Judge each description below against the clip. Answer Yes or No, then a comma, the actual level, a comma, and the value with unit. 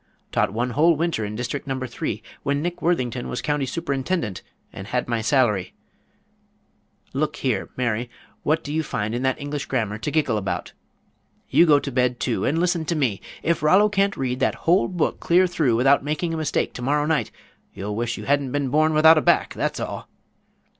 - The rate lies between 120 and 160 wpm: No, average, 195 wpm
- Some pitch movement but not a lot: Yes, average, 4.6 semitones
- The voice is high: No, medium, 140 Hz